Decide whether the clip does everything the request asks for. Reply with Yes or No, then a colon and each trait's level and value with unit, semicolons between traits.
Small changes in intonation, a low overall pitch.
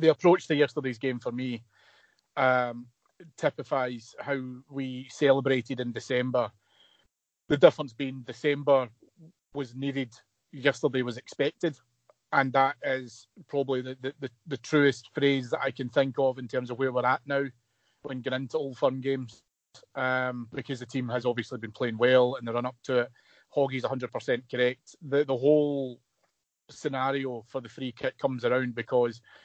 Yes: narrow, 2.0 semitones; low, 130 Hz